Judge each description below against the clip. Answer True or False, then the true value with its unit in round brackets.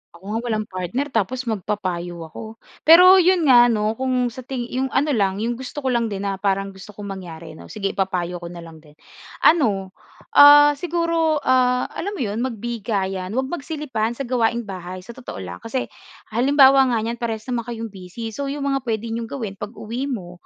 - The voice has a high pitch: True (230 Hz)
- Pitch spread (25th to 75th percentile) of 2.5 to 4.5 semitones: False (5.1 semitones)